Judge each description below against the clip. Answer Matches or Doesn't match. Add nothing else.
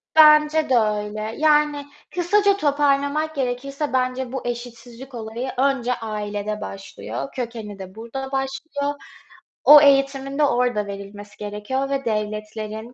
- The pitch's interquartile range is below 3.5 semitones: Doesn't match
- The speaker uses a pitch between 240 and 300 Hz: Matches